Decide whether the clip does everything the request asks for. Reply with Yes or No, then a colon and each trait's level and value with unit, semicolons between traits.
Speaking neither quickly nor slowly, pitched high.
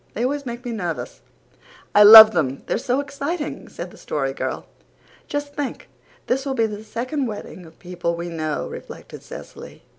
Yes: average, 175 wpm; high, 225 Hz